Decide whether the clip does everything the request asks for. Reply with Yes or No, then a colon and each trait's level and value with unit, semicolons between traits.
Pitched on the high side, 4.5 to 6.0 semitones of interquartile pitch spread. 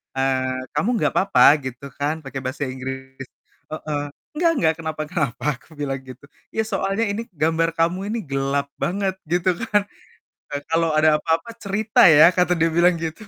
No: medium, 160 Hz; average, 5.1 semitones